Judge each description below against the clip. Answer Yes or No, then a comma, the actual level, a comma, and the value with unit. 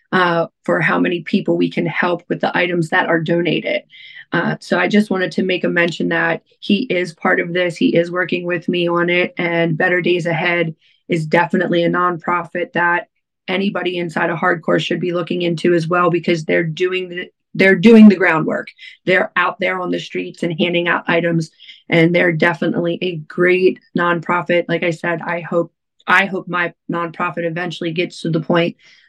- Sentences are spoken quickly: No, average, 190 wpm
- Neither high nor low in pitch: Yes, medium, 175 Hz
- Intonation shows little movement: Yes, narrow, 1.1 semitones